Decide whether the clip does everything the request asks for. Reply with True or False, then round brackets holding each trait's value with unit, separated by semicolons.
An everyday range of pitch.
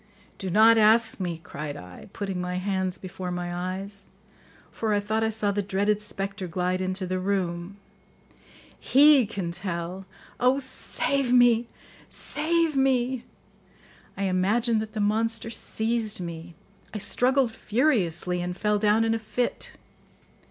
True (3.7 semitones)